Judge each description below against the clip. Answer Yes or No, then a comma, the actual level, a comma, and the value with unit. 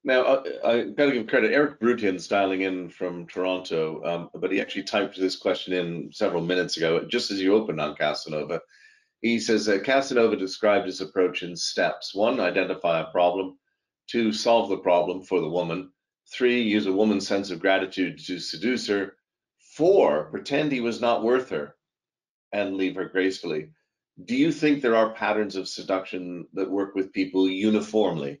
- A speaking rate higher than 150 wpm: Yes, average, 180 wpm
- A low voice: Yes, very low, 95 Hz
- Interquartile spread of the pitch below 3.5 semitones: No, average, 3.8 semitones